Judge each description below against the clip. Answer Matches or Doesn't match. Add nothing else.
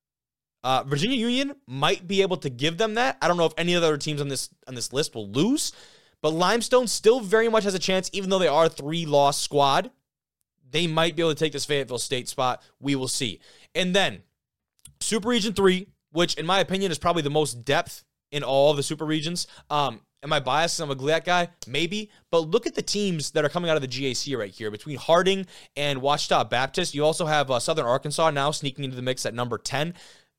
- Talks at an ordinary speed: Doesn't match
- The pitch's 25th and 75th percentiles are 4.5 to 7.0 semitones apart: Matches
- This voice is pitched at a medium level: Matches